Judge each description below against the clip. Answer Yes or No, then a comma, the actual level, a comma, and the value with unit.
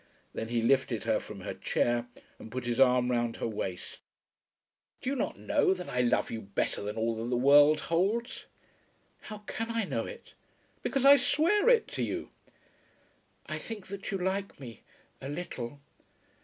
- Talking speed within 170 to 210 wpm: Yes, average, 175 wpm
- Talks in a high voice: No, medium, 140 Hz